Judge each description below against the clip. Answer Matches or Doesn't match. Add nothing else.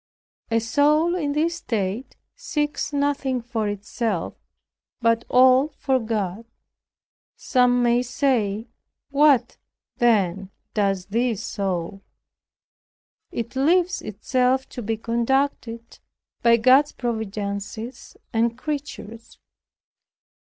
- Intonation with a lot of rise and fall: Doesn't match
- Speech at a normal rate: Doesn't match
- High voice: Matches